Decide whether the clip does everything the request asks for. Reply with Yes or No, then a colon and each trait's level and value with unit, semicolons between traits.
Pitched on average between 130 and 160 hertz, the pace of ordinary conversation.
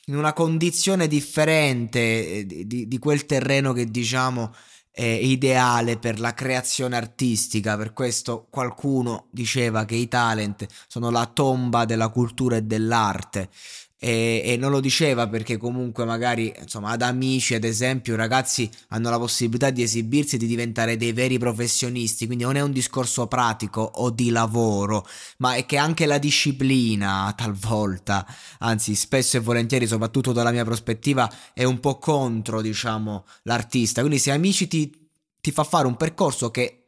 No: low, 120 Hz; average, 160 wpm